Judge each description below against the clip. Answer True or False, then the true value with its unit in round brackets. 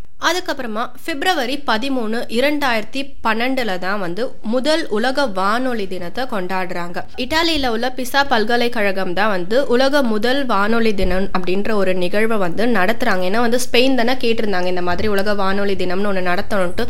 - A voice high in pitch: True (225 Hz)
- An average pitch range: True (4.9 semitones)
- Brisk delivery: True (140 wpm)